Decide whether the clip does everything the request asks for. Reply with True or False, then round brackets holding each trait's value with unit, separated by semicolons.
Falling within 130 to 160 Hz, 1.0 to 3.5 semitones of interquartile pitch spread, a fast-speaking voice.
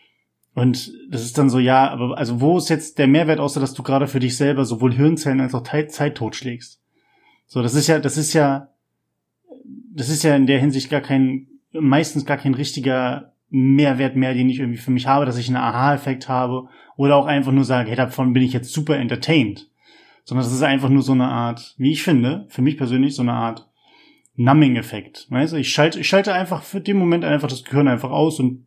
True (135 Hz; 2.6 semitones; 220 wpm)